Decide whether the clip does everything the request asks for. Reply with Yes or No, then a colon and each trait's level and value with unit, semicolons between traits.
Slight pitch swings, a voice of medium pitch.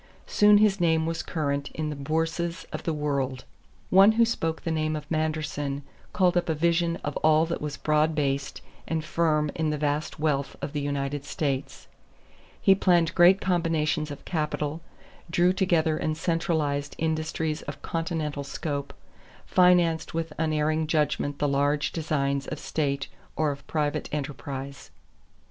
Yes: narrow, 2.2 semitones; medium, 155 Hz